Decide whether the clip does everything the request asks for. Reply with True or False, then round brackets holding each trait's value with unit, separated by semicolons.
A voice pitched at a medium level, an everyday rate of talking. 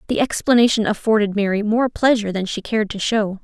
False (215 Hz; 190 wpm)